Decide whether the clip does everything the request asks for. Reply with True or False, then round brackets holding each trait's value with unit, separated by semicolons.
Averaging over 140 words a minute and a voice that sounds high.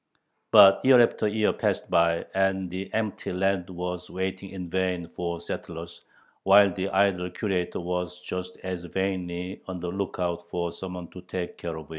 False (165 wpm; 90 Hz)